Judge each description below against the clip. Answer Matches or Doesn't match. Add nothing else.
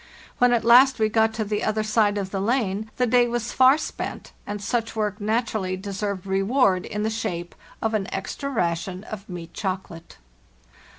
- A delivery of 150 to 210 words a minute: Matches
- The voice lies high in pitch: Matches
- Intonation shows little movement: Doesn't match